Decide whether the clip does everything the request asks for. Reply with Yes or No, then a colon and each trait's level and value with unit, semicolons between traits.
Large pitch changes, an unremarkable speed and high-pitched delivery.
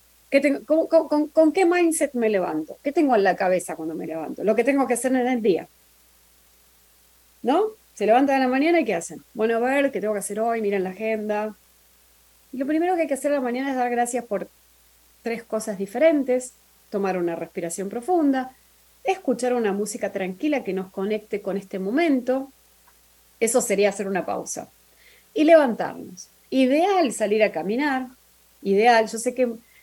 Yes: wide, 6.1 semitones; average, 180 wpm; high, 230 Hz